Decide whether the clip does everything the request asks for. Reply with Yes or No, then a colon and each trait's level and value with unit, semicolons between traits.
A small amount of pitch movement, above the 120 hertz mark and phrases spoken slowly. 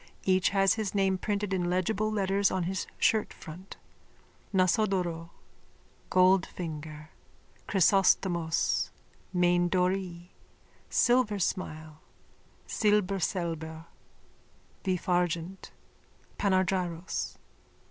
Yes: narrow, 2.2 semitones; medium, 185 Hz; slow, 65 wpm